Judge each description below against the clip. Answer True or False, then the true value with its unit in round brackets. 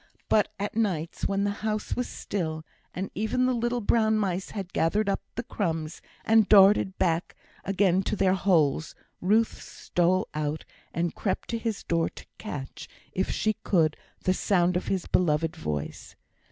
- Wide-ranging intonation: False (4.1 semitones)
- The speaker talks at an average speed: True (160 wpm)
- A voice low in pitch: False (190 Hz)